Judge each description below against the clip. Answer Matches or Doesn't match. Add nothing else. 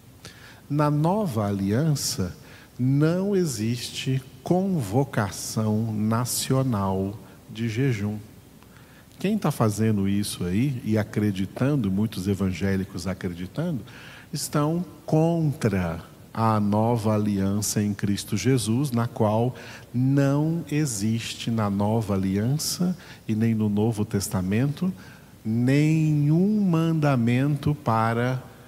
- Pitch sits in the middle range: Doesn't match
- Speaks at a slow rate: Matches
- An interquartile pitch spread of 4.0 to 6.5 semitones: Matches